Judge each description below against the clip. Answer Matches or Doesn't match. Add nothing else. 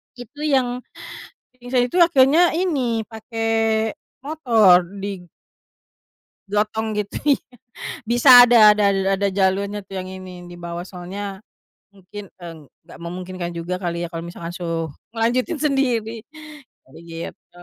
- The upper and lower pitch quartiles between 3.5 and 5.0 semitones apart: Doesn't match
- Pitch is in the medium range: Doesn't match